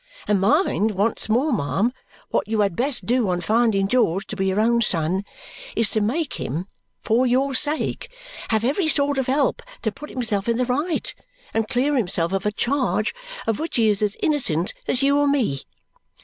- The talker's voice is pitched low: No, high, 230 Hz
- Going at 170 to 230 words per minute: Yes, average, 190 wpm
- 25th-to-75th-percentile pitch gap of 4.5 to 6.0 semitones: Yes, average, 5.1 semitones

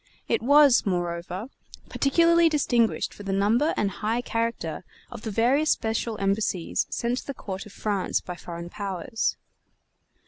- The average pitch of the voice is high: Yes, high, 220 Hz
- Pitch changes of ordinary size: Yes, average, 4.2 semitones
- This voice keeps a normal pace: Yes, average, 145 wpm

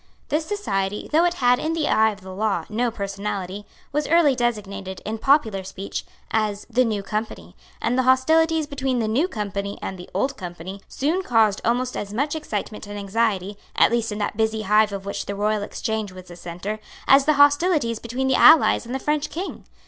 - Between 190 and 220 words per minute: Yes, average, 200 wpm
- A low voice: No, high, 220 Hz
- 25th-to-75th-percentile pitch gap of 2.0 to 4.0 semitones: No, average, 5.1 semitones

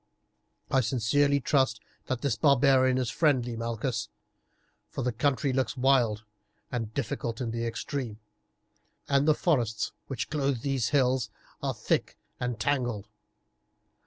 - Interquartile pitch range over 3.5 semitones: No, average, 3.1 semitones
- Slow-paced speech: Yes, slow, 130 wpm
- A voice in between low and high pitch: No, low, 125 Hz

